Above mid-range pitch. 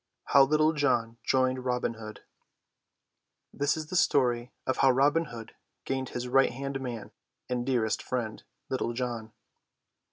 No: low, 130 Hz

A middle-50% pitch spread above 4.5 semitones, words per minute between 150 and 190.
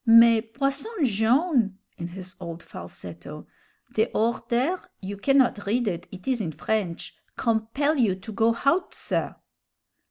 No: wide, 5.5 semitones; slow, 135 wpm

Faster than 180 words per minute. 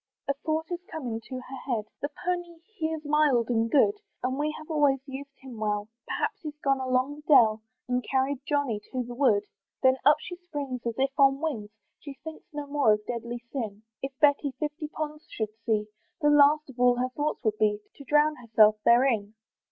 Yes: average, 200 wpm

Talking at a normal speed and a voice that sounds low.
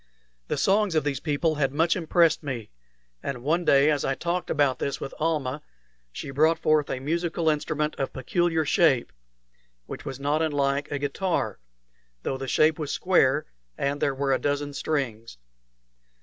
No: average, 165 wpm; medium, 145 Hz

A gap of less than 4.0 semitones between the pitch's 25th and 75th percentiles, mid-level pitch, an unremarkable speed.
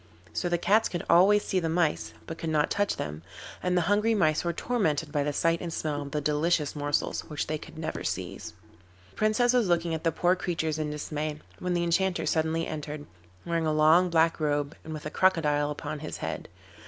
No: average, 2.8 semitones; medium, 160 Hz; fast, 215 wpm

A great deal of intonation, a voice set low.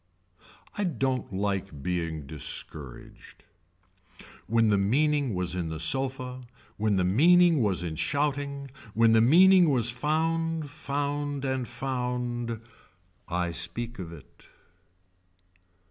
Yes: wide, 7.2 semitones; low, 120 Hz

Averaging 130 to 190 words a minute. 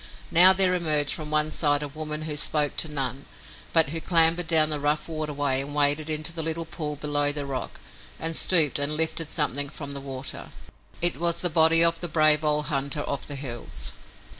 No: average, 200 wpm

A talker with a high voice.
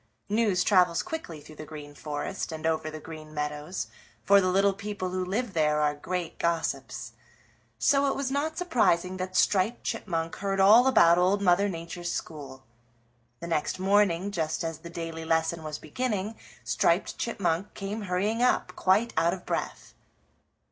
No: medium, 180 Hz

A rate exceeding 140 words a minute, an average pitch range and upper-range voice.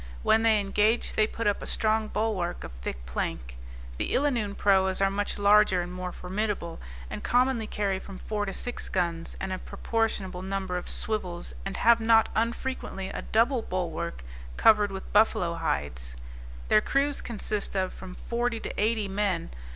Yes: average, 165 wpm; average, 3.5 semitones; high, 200 Hz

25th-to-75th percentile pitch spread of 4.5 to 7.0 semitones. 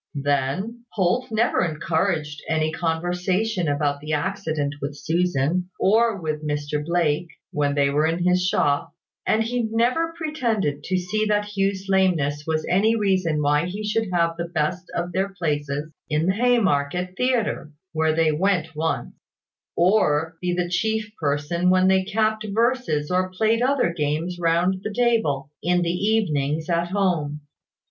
Yes: average, 5.1 semitones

